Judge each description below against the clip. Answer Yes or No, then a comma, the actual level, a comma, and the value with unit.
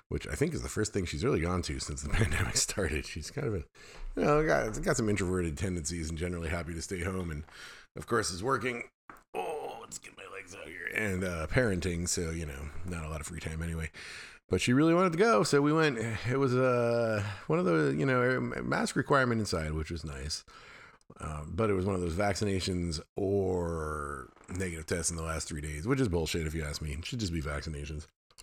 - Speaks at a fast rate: Yes, fast, 230 wpm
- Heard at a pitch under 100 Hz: Yes, very low, 90 Hz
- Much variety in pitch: Yes, wide, 6.4 semitones